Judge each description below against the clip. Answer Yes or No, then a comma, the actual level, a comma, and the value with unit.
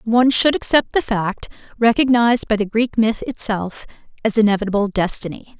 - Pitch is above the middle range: Yes, high, 220 Hz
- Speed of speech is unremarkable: Yes, average, 150 wpm